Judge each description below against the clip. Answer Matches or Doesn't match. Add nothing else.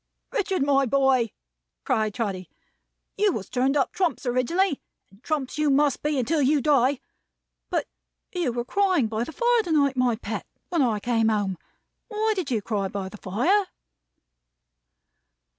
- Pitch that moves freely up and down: Matches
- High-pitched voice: Matches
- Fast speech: Doesn't match